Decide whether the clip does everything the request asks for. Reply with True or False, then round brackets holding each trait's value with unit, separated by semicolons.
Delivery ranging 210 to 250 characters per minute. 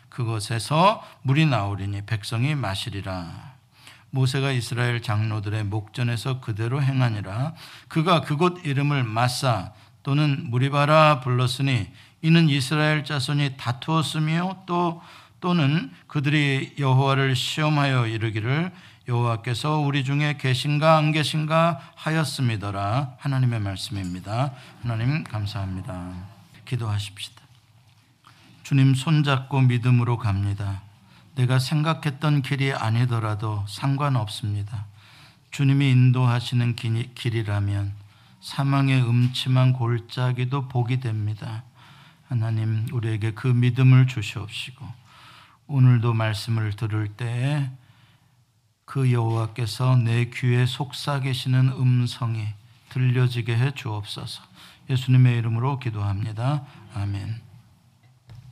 False (265 characters per minute)